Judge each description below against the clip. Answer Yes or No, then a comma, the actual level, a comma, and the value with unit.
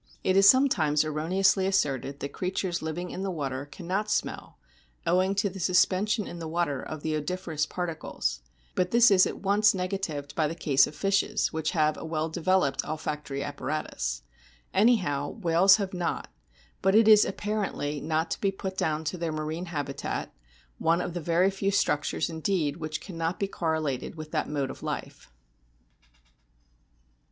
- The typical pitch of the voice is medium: Yes, medium, 170 Hz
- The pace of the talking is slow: No, average, 165 wpm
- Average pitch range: Yes, average, 4.0 semitones